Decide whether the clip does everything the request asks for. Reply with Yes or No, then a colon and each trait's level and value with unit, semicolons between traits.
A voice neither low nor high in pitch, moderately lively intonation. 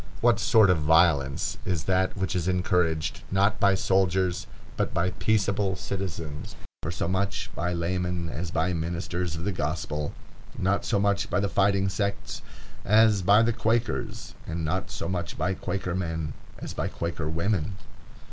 No: very low, 90 Hz; average, 3.0 semitones